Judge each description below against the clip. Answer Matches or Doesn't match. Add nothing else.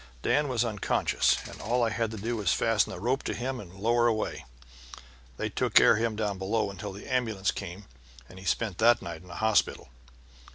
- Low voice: Matches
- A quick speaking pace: Matches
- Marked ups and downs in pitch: Doesn't match